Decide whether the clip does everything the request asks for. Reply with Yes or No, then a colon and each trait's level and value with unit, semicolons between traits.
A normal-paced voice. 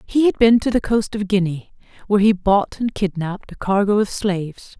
No: fast, 215 wpm